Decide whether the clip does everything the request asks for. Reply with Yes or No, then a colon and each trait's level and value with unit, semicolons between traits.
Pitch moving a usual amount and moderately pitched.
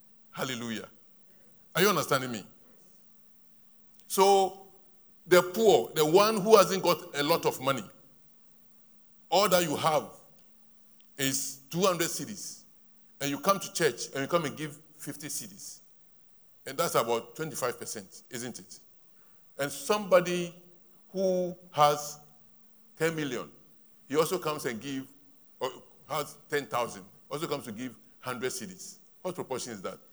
No: wide, 5.7 semitones; medium, 170 Hz